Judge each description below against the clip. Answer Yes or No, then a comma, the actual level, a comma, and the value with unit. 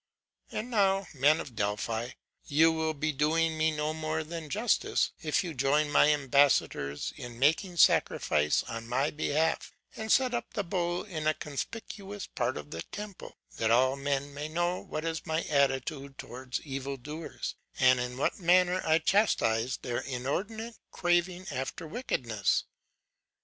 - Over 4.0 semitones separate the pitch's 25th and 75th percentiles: Yes, average, 4.7 semitones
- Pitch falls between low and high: Yes, medium, 155 Hz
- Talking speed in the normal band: Yes, average, 155 wpm